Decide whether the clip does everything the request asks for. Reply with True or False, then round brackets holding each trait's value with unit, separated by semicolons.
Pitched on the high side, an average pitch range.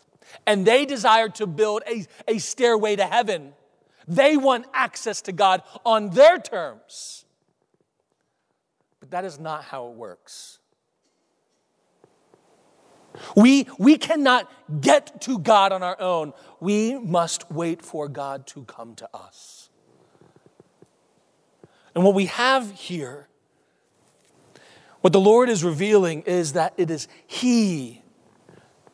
False (200 Hz; 5.8 semitones)